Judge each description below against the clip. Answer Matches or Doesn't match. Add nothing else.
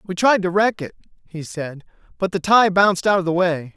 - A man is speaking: Matches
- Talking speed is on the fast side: Matches